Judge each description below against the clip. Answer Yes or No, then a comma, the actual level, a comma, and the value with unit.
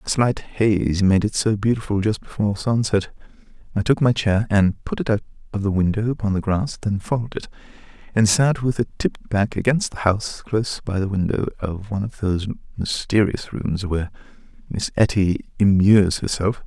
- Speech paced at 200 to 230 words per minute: No, average, 185 wpm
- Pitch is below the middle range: Yes, low, 105 Hz